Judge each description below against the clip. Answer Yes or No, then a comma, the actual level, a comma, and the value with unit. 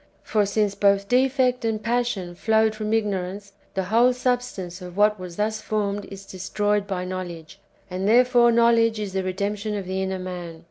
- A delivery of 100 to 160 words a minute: No, average, 175 wpm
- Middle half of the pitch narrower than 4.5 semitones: Yes, average, 3.1 semitones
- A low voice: No, high, 205 Hz